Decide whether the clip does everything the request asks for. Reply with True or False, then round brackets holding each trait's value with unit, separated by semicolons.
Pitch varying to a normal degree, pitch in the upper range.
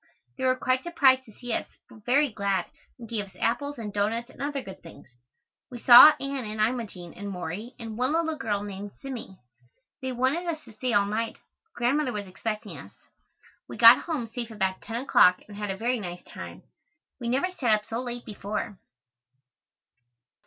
True (4.0 semitones; 230 Hz)